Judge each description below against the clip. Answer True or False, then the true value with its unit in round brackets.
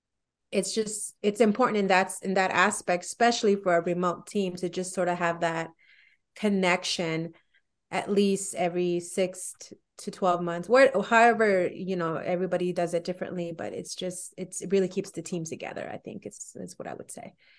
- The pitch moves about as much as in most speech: False (2.3 semitones)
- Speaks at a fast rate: False (190 wpm)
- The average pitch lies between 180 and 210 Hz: True (185 Hz)